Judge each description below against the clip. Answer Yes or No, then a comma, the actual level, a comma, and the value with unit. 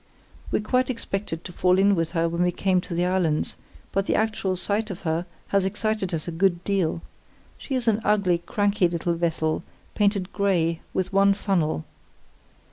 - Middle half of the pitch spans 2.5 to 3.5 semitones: Yes, average, 3.0 semitones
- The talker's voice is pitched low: No, medium, 185 Hz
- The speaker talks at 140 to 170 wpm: No, average, 180 wpm